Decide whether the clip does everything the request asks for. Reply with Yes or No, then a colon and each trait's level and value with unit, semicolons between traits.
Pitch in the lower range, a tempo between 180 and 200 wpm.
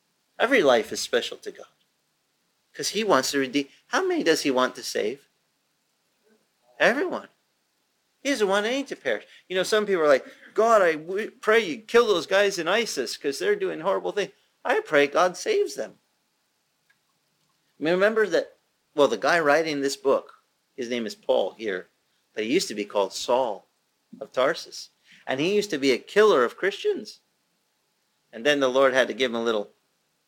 No: high, 205 Hz; average, 185 wpm